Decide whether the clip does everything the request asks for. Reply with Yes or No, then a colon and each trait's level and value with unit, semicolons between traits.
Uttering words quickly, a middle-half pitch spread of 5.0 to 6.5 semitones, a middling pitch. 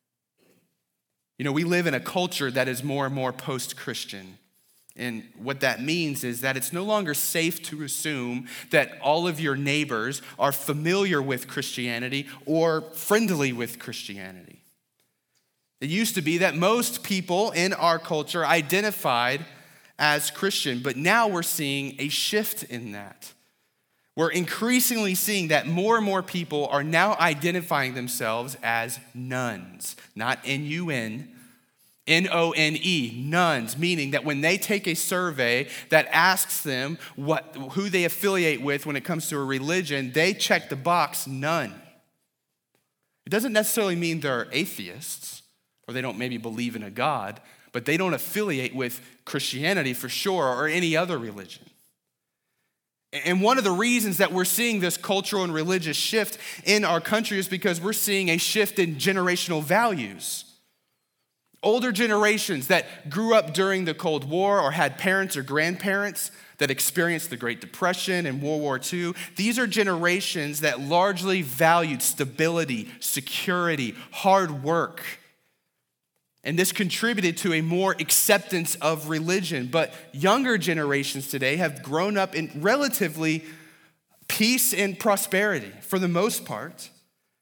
No: average, 150 wpm; average, 5.3 semitones; medium, 165 Hz